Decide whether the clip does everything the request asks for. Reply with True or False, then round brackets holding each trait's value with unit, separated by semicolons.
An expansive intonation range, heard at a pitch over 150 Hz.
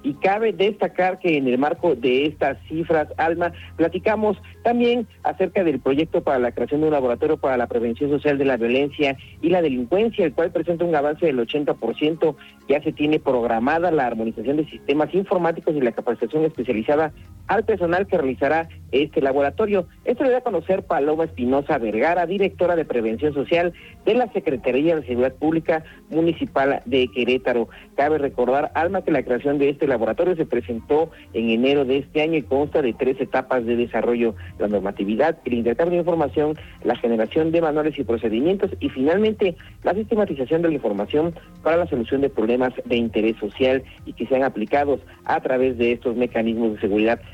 False (5.7 semitones; 145 Hz)